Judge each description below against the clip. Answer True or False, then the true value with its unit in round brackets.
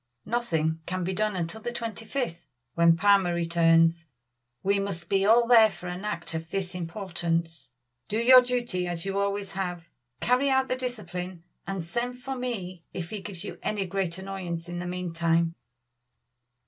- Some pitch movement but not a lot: True (4.0 semitones)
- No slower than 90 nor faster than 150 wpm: False (170 wpm)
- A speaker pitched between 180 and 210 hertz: True (185 Hz)